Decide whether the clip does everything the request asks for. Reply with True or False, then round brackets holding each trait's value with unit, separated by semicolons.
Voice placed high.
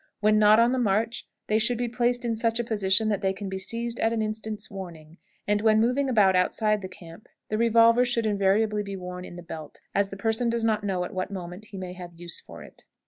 True (210 Hz)